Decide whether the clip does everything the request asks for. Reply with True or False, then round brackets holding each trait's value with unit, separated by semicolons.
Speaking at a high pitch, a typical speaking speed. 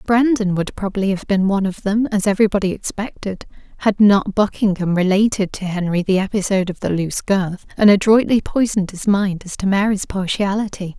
True (200 Hz; 175 wpm)